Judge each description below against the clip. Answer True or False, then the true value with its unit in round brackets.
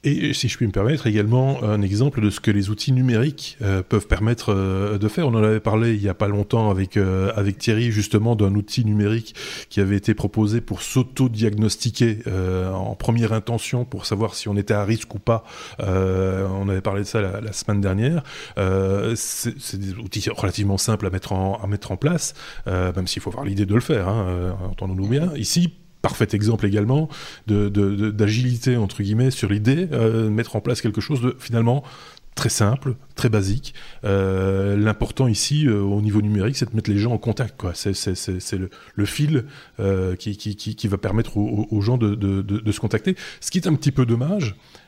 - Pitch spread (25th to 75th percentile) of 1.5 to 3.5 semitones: True (3.2 semitones)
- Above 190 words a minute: True (215 wpm)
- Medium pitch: False (110 Hz)